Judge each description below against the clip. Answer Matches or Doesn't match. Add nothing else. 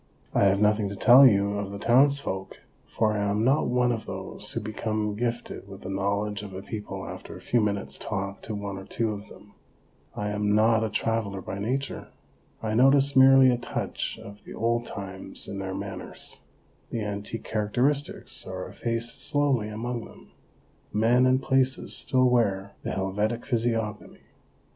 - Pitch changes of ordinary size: Matches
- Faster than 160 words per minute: Matches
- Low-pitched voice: Matches